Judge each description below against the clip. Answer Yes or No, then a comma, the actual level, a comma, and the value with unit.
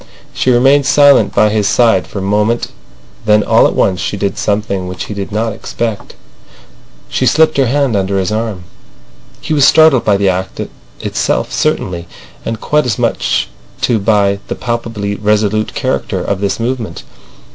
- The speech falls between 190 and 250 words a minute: No, average, 165 wpm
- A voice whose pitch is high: No, low, 105 Hz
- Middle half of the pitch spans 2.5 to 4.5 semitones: Yes, average, 3.1 semitones